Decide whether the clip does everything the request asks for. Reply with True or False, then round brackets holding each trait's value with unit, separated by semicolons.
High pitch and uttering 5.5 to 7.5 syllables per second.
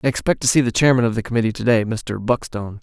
False (115 Hz; 7.0 syllables/s)